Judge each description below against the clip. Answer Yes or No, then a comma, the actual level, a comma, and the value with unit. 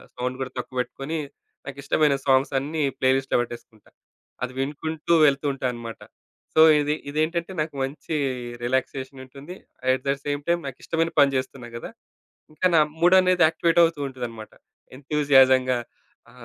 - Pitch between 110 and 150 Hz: Yes, medium, 140 Hz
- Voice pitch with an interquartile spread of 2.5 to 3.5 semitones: Yes, average, 3.2 semitones